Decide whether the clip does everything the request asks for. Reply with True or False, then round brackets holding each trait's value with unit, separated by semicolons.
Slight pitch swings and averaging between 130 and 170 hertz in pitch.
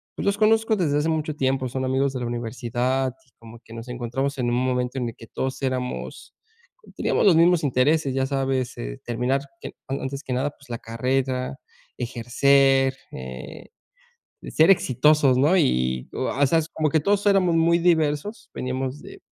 False (3.4 semitones; 135 Hz)